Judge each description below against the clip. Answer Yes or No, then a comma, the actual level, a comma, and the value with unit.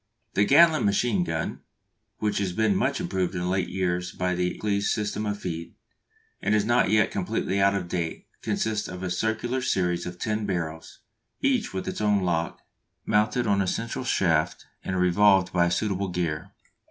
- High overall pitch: No, very low, 95 Hz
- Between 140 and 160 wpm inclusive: No, average, 175 wpm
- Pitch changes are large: No, average, 3.2 semitones